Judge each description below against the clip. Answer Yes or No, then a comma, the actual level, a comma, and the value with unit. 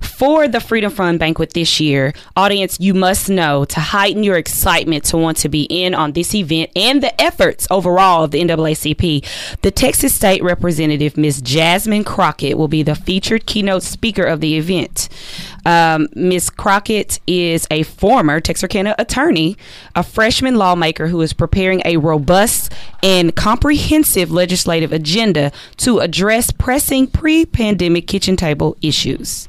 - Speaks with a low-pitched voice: No, medium, 175 Hz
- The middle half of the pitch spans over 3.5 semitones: Yes, average, 3.9 semitones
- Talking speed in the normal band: Yes, average, 150 wpm